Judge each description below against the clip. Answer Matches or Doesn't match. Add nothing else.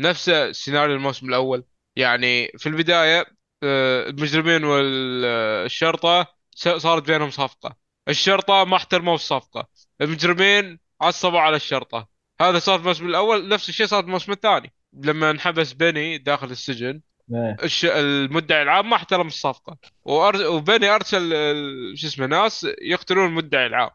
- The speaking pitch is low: Doesn't match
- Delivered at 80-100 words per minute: Doesn't match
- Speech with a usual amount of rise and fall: Matches